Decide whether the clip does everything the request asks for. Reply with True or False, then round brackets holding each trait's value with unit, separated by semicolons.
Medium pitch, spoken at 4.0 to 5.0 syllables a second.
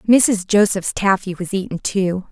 False (195 Hz; 4.3 syllables/s)